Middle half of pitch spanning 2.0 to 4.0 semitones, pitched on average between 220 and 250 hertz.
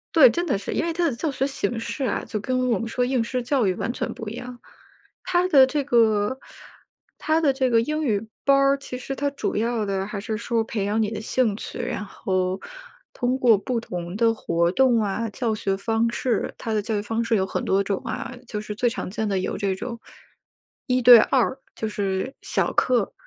Yes: average, 3.7 semitones; high, 230 Hz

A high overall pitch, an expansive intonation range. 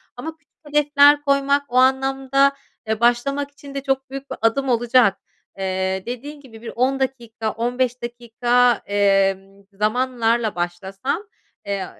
No: high, 245 Hz; average, 3.9 semitones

